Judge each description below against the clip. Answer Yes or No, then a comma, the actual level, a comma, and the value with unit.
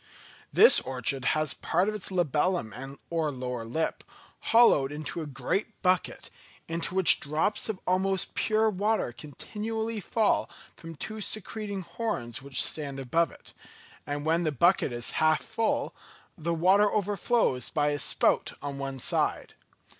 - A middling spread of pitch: No, wide, 6.3 semitones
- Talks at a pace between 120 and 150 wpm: Yes, average, 145 wpm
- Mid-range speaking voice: Yes, medium, 165 Hz